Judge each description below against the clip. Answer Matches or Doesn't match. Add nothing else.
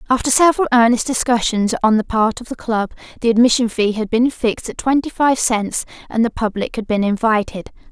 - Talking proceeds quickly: Doesn't match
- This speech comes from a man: Doesn't match